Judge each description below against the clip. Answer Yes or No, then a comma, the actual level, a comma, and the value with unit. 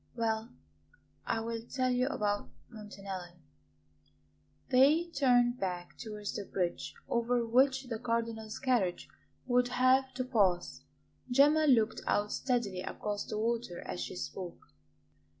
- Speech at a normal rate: No, slow, 125 wpm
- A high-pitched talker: Yes, high, 230 Hz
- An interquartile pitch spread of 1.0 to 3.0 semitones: No, average, 3.7 semitones